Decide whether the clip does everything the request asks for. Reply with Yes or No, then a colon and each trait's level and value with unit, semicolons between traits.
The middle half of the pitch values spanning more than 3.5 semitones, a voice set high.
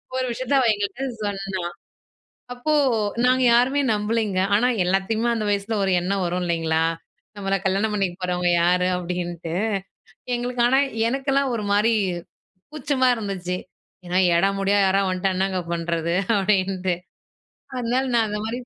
Yes: average, 4.6 semitones; high, 200 Hz